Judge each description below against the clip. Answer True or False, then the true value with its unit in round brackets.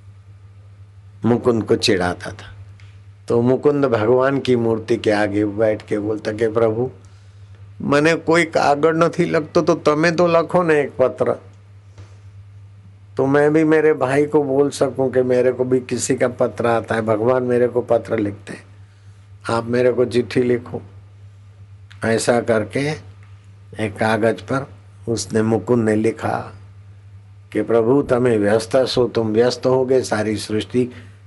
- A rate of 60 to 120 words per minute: False (145 wpm)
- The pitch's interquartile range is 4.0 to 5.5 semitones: True (4.3 semitones)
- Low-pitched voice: True (115 Hz)